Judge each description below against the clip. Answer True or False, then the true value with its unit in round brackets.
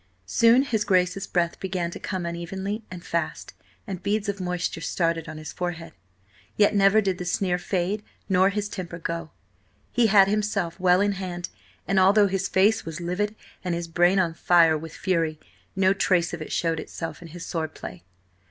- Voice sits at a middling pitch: True (180 Hz)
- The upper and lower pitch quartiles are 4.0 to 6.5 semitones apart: False (2.7 semitones)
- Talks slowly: False (185 wpm)